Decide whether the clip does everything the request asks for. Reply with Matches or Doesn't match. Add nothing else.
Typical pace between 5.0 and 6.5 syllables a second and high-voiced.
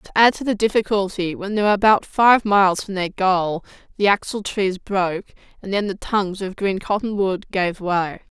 Matches